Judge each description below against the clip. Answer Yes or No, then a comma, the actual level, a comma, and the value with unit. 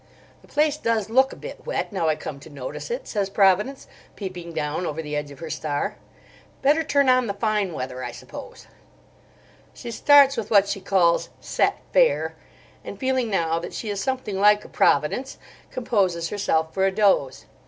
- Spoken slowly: No, average, 180 wpm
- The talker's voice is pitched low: No, high, 200 Hz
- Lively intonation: Yes, wide, 7.3 semitones